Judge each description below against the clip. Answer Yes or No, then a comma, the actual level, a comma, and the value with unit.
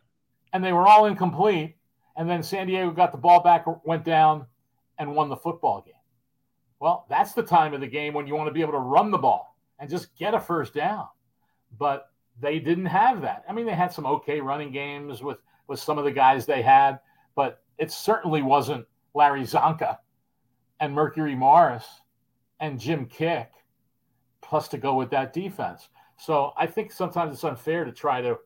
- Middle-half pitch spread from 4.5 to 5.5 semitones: No, average, 3.6 semitones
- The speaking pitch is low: No, medium, 155 Hz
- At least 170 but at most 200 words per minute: Yes, average, 190 wpm